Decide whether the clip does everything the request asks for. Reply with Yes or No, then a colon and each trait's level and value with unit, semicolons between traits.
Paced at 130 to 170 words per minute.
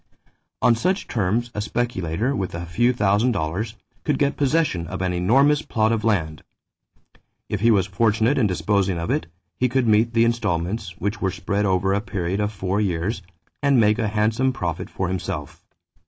No: average, 180 wpm